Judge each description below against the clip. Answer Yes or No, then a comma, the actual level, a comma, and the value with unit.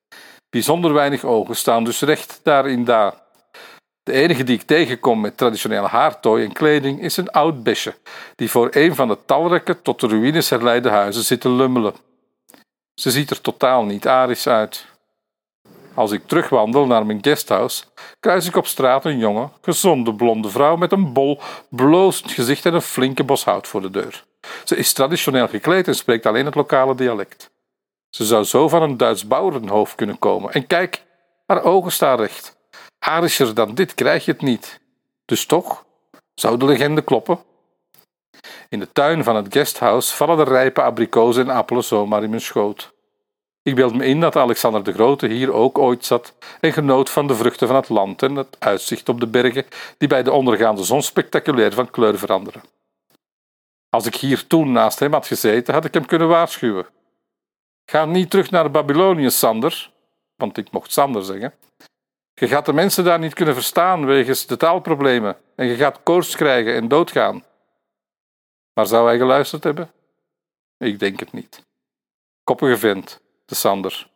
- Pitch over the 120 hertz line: Yes, low, 135 Hz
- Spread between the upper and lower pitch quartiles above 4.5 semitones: Yes, average, 5.1 semitones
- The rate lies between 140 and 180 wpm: Yes, average, 175 wpm